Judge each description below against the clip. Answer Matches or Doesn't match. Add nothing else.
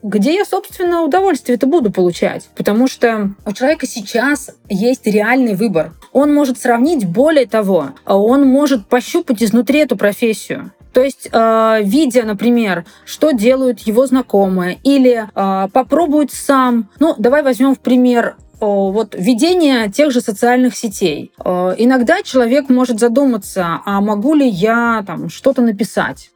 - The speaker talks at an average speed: Matches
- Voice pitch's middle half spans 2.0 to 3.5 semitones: Doesn't match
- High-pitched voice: Matches